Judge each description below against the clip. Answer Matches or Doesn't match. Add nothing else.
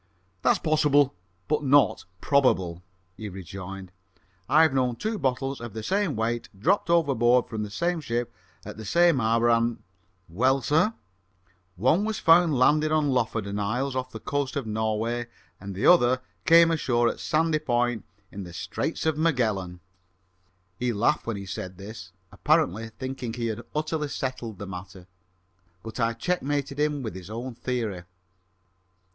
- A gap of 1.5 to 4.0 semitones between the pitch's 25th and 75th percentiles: Doesn't match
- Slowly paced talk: Doesn't match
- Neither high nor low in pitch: Doesn't match